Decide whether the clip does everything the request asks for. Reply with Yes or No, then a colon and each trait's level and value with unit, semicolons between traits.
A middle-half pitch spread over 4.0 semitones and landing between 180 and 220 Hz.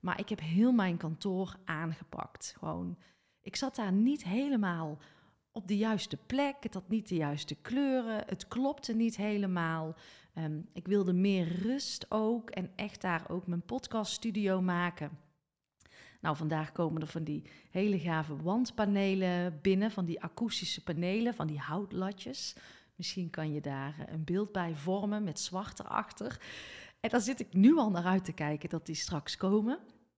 Yes: average, 4.7 semitones; medium, 185 Hz